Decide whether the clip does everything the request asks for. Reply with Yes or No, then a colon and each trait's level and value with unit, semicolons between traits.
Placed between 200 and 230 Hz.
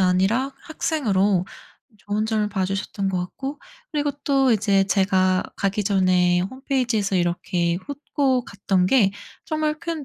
Yes: high, 205 Hz